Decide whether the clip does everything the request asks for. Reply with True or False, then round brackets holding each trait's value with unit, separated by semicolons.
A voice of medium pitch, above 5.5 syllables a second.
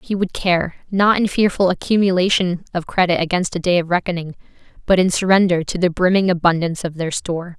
True (180 Hz; 5.9 syllables/s)